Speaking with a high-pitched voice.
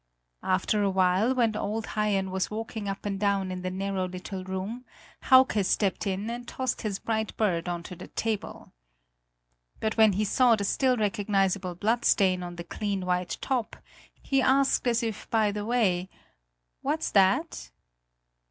Yes: high, 205 Hz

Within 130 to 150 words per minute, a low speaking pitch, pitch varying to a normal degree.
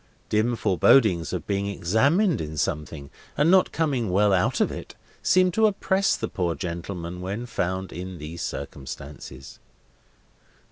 No: average, 140 wpm; very low, 95 Hz; wide, 7.3 semitones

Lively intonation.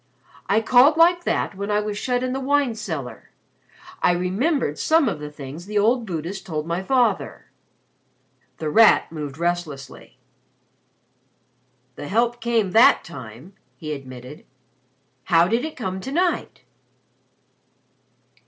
Yes: wide, 7.8 semitones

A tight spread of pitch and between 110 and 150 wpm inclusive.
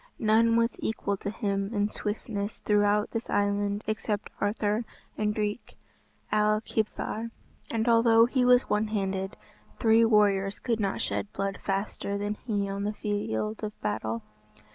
Yes: narrow, 1.6 semitones; average, 145 wpm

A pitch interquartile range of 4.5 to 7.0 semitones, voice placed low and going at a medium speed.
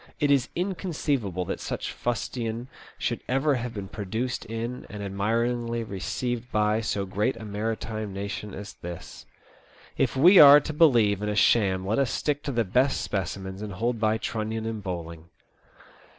No: average, 3.5 semitones; low, 110 Hz; average, 165 wpm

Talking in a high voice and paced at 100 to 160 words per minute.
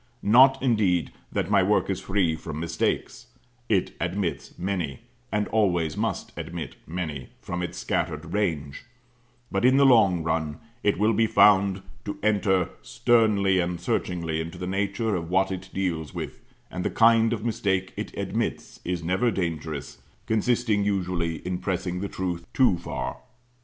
No: very low, 95 Hz; average, 155 wpm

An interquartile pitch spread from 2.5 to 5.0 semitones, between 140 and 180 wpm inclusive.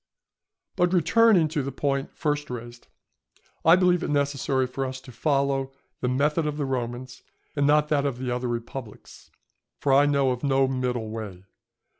Yes: average, 2.8 semitones; average, 170 wpm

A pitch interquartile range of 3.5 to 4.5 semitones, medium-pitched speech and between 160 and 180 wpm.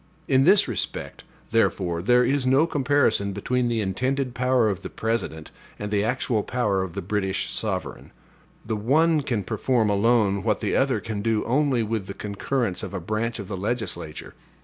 No: average, 4.1 semitones; low, 115 Hz; average, 175 wpm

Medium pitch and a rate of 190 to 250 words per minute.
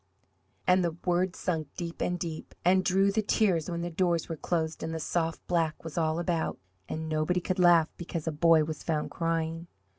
Yes: medium, 170 Hz; average, 200 wpm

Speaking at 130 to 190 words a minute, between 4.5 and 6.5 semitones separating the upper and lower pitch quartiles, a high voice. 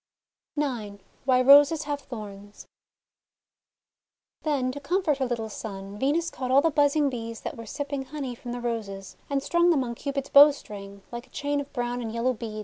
No: average, 180 wpm; average, 4.0 semitones; very high, 255 Hz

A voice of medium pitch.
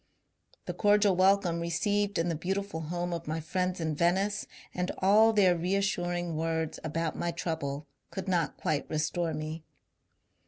Yes: medium, 175 Hz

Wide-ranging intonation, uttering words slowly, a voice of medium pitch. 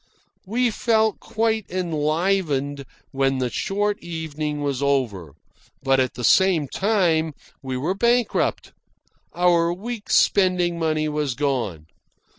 Yes: wide, 5.8 semitones; slow, 115 wpm; medium, 160 Hz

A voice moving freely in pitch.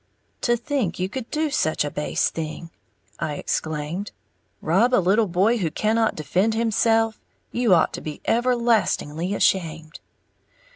Yes: wide, 6.1 semitones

